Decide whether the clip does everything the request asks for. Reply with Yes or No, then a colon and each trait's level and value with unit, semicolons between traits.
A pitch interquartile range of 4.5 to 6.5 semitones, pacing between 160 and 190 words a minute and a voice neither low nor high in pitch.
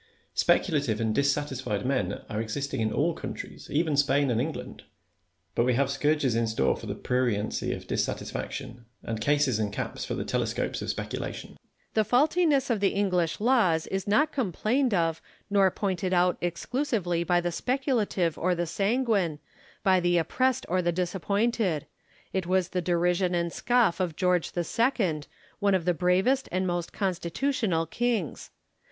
Yes: wide, 5.6 semitones; average, 165 wpm; medium, 175 Hz